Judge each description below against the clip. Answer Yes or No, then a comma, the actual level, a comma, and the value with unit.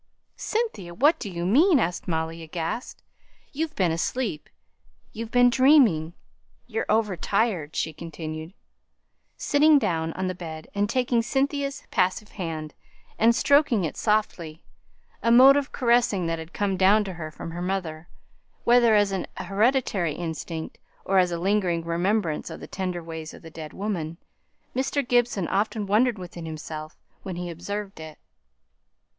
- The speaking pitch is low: No, high, 190 Hz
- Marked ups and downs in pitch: Yes, wide, 5.9 semitones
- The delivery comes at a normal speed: Yes, average, 150 wpm